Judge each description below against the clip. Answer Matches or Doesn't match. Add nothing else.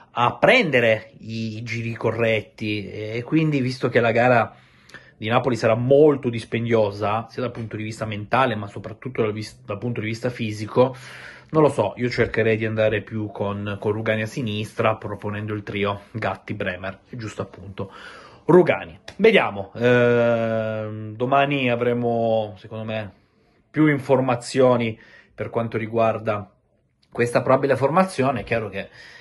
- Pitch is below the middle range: Matches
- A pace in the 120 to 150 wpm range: Matches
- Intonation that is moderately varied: Doesn't match